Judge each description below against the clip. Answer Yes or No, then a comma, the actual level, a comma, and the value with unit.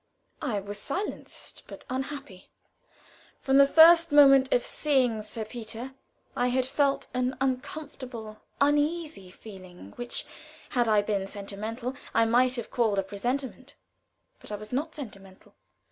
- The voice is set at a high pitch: Yes, high, 245 Hz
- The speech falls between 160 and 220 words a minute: No, slow, 135 wpm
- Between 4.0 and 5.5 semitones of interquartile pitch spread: Yes, average, 4.6 semitones